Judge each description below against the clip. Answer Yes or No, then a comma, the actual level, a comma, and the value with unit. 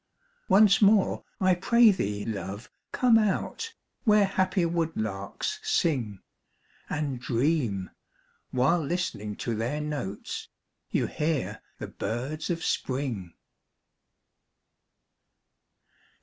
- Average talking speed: No, slow, 90 wpm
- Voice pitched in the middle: Yes, medium, 150 Hz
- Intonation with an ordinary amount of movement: No, wide, 8.8 semitones